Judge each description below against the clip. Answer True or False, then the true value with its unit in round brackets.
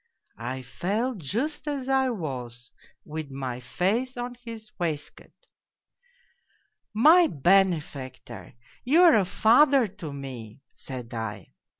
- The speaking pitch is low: False (185 Hz)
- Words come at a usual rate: False (125 wpm)